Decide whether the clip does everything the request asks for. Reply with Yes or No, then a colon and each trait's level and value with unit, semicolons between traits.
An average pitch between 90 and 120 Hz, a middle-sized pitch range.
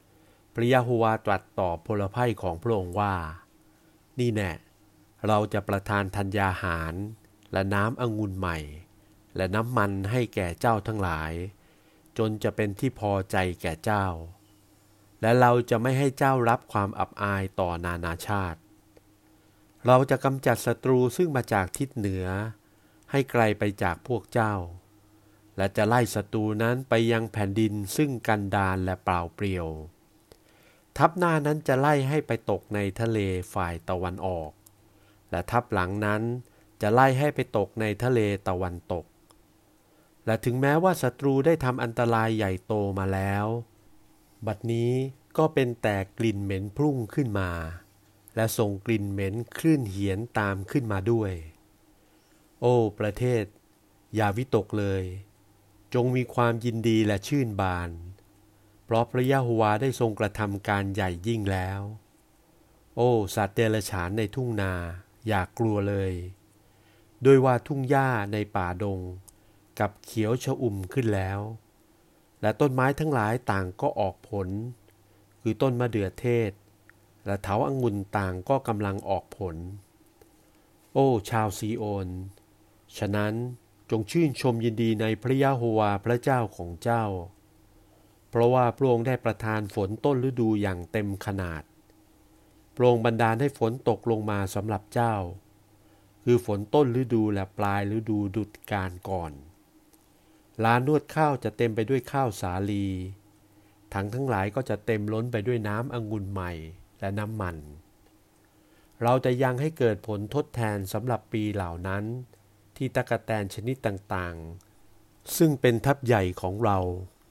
Yes: low, 105 Hz; average, 3.1 semitones